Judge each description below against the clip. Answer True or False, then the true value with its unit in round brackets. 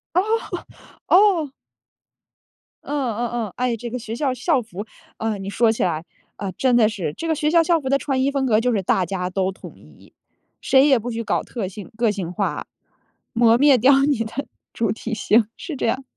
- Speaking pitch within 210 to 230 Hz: False (240 Hz)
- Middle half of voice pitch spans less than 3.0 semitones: False (4.7 semitones)